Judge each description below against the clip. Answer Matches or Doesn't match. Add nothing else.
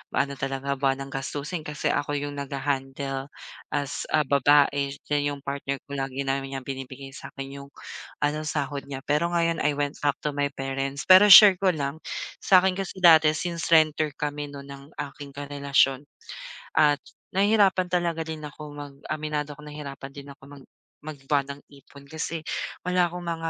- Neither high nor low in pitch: Matches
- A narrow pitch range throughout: Matches